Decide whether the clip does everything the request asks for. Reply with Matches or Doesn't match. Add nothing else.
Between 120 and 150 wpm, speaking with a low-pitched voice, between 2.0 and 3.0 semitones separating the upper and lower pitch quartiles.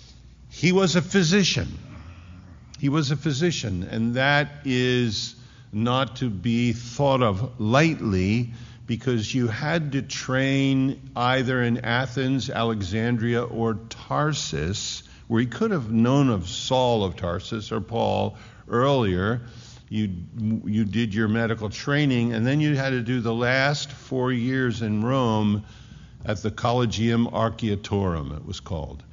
Doesn't match